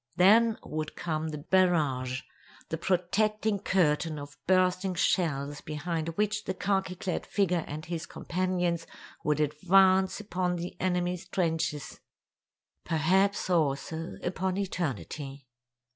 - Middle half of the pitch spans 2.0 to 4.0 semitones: Yes, average, 3.4 semitones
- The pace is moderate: No, slow, 105 wpm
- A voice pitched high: No, medium, 175 Hz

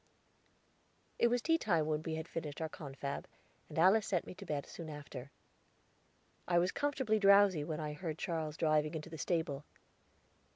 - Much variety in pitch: No, average, 3.6 semitones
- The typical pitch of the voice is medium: Yes, medium, 160 Hz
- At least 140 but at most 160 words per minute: No, average, 170 wpm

